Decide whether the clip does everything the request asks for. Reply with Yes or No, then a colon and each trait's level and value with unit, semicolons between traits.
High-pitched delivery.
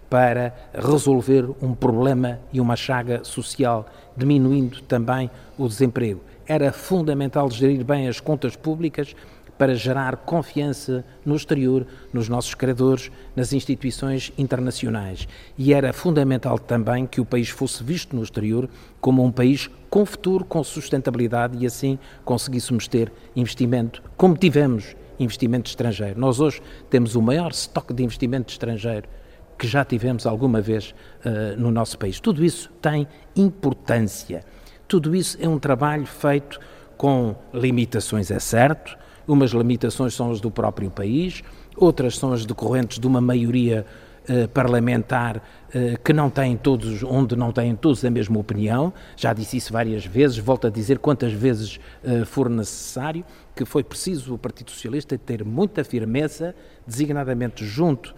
No: low, 130 Hz